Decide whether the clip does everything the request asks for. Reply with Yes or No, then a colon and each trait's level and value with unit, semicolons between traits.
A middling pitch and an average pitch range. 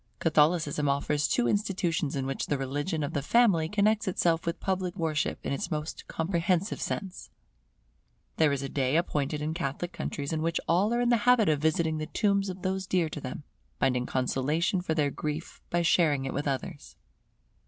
Yes: medium, 160 Hz; average, 4.2 semitones